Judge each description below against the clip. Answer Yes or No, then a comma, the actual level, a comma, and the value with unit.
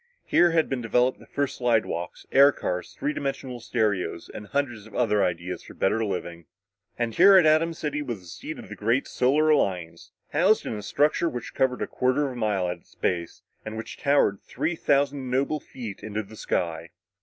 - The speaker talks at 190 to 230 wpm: Yes, average, 200 wpm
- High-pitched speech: No, low, 120 Hz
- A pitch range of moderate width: No, wide, 5.8 semitones